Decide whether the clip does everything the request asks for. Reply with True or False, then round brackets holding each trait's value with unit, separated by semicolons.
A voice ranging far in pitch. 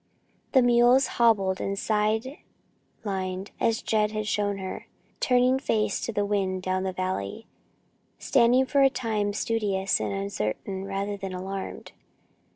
False (3.1 semitones)